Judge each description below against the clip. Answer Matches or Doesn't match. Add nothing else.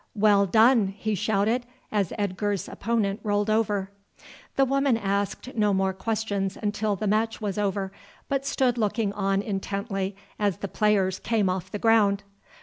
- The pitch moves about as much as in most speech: Doesn't match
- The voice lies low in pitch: Doesn't match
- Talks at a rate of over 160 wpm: Doesn't match